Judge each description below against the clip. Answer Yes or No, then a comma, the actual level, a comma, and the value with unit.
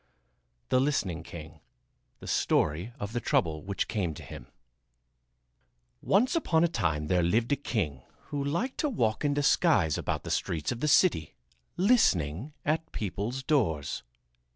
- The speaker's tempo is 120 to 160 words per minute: Yes, average, 150 wpm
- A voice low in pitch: Yes, low, 115 Hz